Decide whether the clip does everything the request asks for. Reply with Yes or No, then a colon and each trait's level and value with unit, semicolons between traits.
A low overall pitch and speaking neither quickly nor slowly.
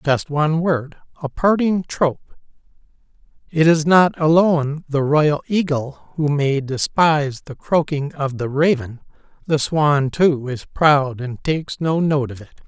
No: medium, 150 Hz; average, 150 wpm